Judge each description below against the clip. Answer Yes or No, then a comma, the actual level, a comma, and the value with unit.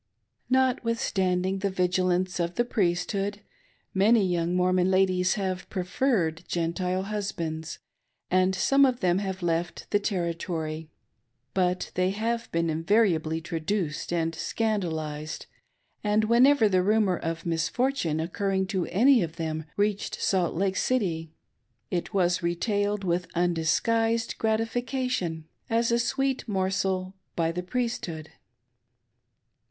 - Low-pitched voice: No, medium, 185 Hz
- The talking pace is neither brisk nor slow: No, slow, 115 wpm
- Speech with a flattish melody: No, average, 3.8 semitones